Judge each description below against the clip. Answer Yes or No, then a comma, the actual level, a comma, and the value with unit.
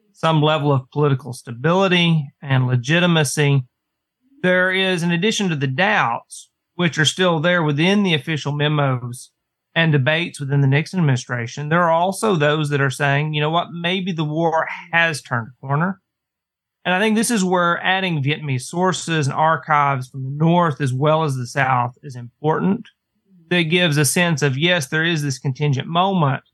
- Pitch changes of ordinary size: Yes, average, 4.0 semitones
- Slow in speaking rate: No, average, 175 wpm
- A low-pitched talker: No, medium, 155 Hz